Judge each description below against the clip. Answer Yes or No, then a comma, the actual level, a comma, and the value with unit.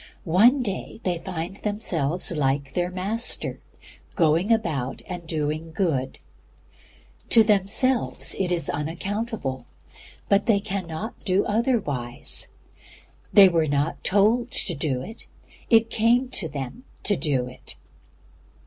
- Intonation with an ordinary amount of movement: No, wide, 6.0 semitones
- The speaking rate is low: Yes, slow, 120 wpm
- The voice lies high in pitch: No, medium, 180 Hz